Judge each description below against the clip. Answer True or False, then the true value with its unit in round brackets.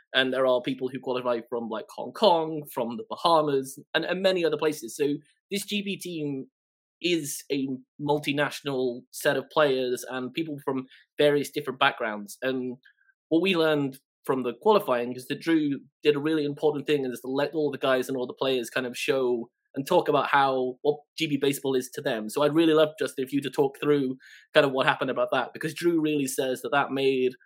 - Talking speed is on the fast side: True (210 wpm)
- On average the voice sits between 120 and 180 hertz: True (140 Hz)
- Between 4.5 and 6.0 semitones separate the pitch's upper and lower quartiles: False (3.1 semitones)